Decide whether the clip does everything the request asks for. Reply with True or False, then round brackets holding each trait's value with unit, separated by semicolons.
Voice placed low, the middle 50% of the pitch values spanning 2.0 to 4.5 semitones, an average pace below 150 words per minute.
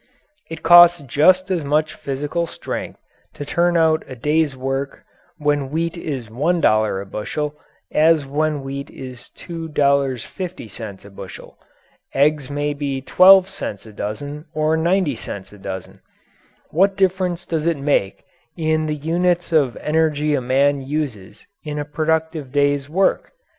False (150 Hz; 3.3 semitones; 140 wpm)